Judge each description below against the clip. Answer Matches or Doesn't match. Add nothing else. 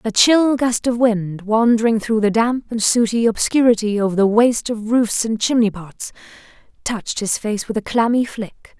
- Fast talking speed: Doesn't match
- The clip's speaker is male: Doesn't match